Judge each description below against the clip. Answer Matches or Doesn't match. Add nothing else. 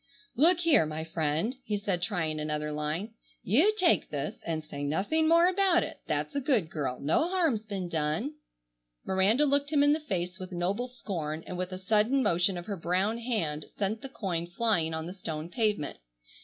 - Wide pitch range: Matches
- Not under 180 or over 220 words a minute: Matches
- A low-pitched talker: Doesn't match